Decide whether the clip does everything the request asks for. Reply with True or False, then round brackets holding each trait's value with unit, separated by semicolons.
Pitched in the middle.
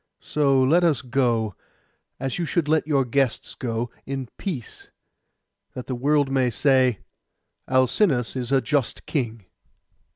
False (130 Hz)